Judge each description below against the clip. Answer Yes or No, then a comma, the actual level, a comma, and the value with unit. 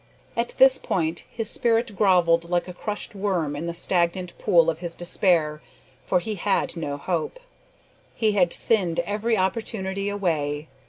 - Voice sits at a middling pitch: Yes, medium, 180 Hz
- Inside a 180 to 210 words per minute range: No, average, 155 wpm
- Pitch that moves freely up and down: No, average, 3.6 semitones